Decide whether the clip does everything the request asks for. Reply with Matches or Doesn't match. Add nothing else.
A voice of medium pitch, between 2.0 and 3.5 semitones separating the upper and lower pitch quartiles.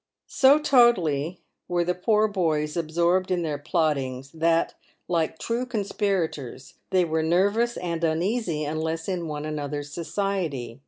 Doesn't match